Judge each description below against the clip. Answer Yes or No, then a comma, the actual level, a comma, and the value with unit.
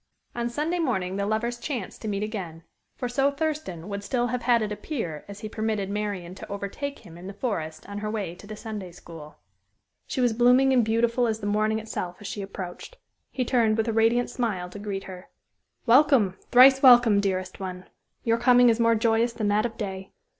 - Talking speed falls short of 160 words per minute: No, fast, 205 wpm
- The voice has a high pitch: Yes, high, 215 Hz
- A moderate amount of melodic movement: Yes, average, 3.7 semitones